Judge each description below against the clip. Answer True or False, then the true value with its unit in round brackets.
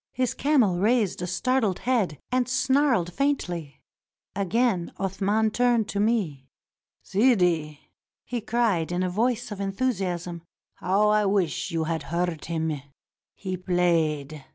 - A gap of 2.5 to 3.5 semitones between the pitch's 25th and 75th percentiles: False (5.5 semitones)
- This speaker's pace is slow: True (130 wpm)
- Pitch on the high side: True (195 Hz)